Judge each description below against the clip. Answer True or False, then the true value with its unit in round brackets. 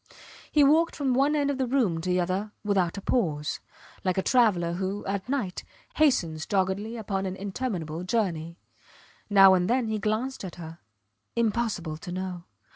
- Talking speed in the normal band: True (170 wpm)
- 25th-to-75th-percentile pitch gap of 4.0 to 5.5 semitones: True (4.9 semitones)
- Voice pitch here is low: False (195 Hz)